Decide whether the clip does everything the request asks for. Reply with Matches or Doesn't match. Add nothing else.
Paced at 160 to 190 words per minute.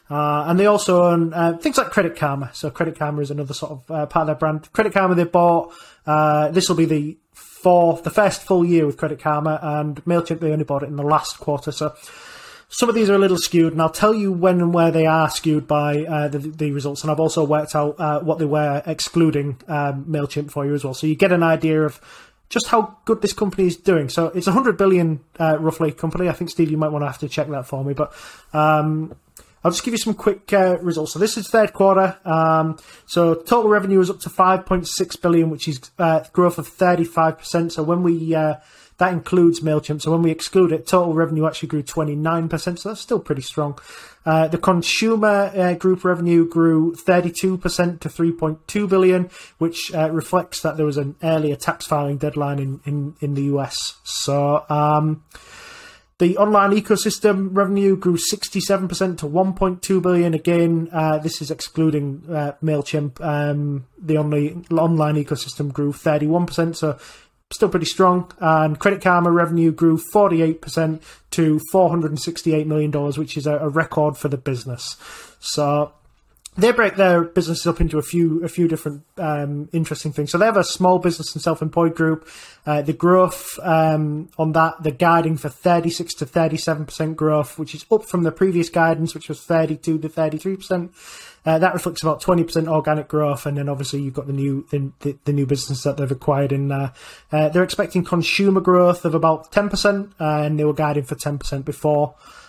Doesn't match